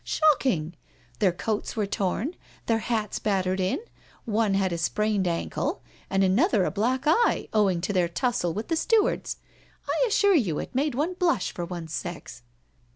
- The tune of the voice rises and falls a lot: Yes, wide, 6.7 semitones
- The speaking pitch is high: Yes, high, 210 Hz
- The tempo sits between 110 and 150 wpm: No, average, 165 wpm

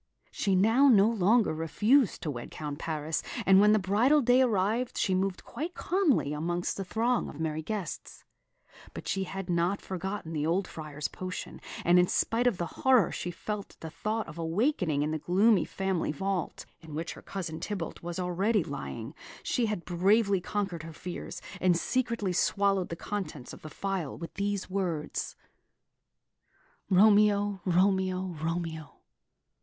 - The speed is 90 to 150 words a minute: No, average, 160 wpm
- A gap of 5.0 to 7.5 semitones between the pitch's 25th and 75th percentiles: No, average, 3.9 semitones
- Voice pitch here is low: No, high, 190 Hz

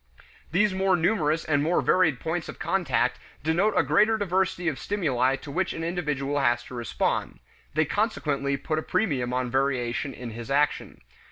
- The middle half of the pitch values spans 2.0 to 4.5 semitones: No, average, 5.1 semitones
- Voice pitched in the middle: Yes, medium, 150 Hz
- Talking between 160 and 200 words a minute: Yes, average, 170 wpm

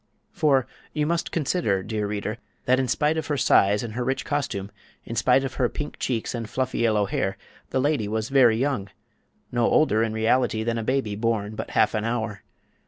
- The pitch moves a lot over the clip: No, average, 3.7 semitones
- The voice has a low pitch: Yes, low, 115 Hz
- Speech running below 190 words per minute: No, average, 195 wpm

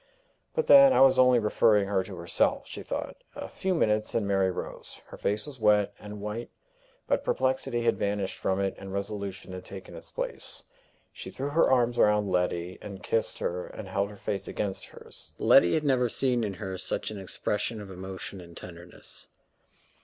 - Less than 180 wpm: No, average, 190 wpm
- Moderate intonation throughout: Yes, average, 3.9 semitones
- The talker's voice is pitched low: Yes, low, 105 Hz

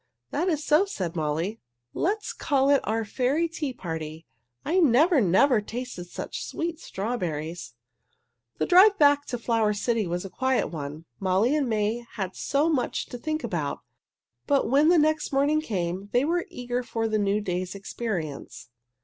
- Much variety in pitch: Yes, wide, 7.8 semitones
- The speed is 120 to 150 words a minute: No, average, 165 wpm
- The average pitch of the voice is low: No, high, 240 Hz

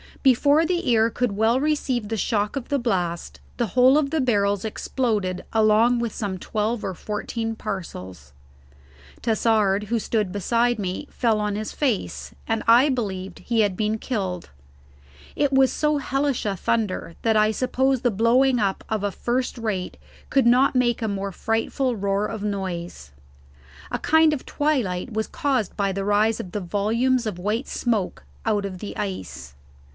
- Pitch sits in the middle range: No, high, 220 Hz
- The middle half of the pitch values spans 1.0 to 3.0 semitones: No, average, 3.8 semitones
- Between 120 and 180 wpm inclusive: Yes, average, 170 wpm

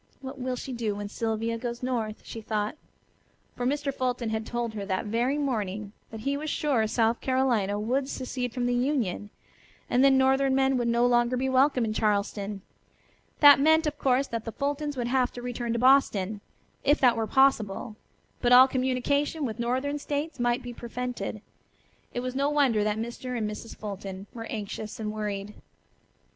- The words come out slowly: No, average, 180 wpm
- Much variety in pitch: No, average, 3.4 semitones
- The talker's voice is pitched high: Yes, high, 245 Hz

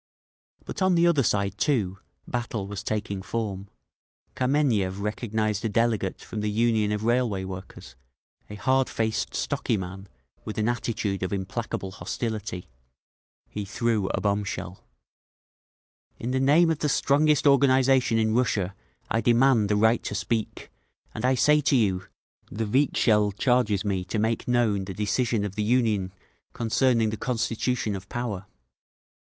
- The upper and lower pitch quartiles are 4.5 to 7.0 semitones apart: No, average, 3.5 semitones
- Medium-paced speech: Yes, average, 145 wpm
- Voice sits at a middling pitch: No, low, 110 Hz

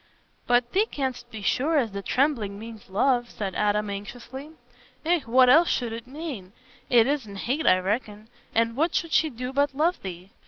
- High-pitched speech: Yes, high, 240 Hz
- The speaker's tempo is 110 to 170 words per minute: No, average, 185 wpm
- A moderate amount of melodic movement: Yes, average, 5.0 semitones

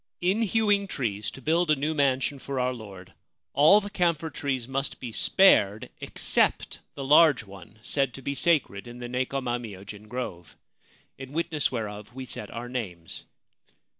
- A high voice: No, low, 130 Hz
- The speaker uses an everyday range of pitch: No, wide, 5.8 semitones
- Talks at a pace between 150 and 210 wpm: Yes, average, 165 wpm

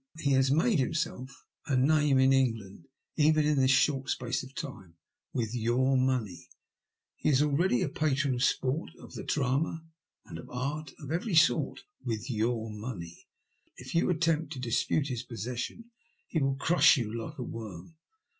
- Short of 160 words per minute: No, average, 175 wpm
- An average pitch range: Yes, average, 3.9 semitones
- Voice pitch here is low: Yes, low, 130 Hz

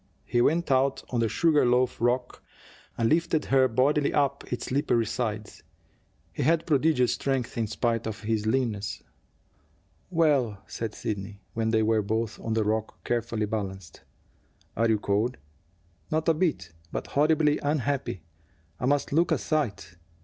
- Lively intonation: No, average, 4.6 semitones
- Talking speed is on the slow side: No, average, 150 wpm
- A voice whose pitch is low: Yes, low, 120 Hz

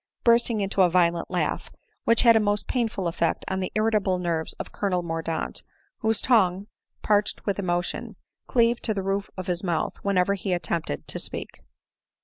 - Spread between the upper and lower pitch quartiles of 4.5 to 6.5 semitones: No, average, 3.4 semitones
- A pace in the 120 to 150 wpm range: No, average, 175 wpm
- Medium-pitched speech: No, high, 195 Hz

